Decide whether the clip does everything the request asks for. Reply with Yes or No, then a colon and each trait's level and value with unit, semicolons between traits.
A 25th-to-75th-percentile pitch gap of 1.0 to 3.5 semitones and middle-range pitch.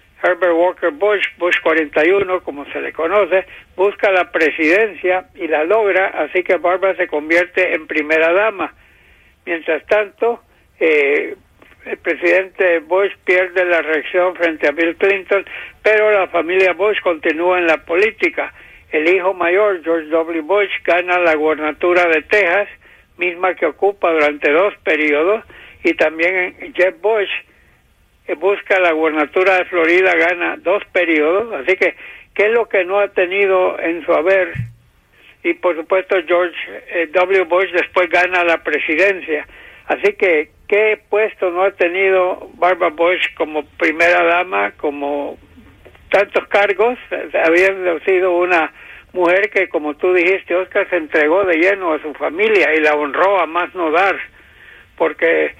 Yes: average, 2.8 semitones; medium, 180 Hz